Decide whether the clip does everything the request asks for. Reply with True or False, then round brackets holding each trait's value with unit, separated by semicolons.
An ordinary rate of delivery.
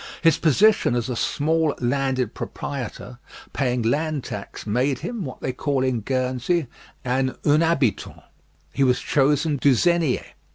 False (130 wpm)